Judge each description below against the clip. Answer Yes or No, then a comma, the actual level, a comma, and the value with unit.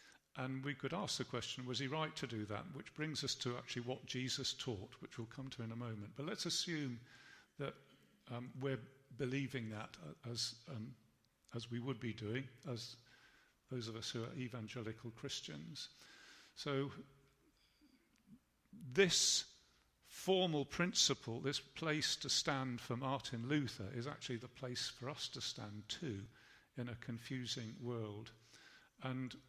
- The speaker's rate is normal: Yes, average, 155 wpm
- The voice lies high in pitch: No, low, 130 Hz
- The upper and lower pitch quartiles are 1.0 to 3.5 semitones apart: Yes, average, 3.0 semitones